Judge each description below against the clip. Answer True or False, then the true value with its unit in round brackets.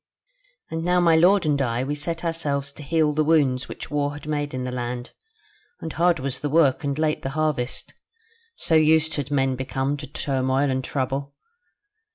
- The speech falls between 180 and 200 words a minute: True (190 wpm)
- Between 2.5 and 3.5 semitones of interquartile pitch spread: True (2.9 semitones)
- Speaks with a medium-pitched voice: True (145 Hz)